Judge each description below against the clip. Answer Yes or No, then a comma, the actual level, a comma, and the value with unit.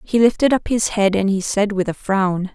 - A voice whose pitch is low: No, high, 205 Hz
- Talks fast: Yes, fast, 260 wpm